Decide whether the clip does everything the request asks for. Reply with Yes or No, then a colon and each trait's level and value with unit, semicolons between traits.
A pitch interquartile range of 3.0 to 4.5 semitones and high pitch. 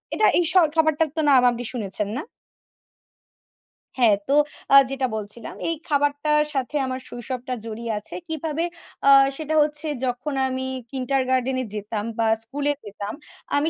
Yes: average, 3.9 semitones; very high, 260 Hz